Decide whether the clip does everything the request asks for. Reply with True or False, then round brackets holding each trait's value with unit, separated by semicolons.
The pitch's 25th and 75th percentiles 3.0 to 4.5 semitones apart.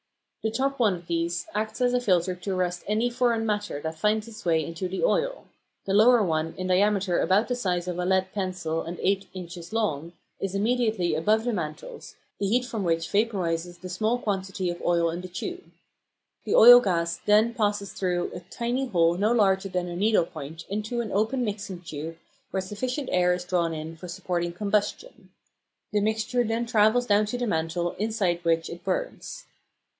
True (4.1 semitones)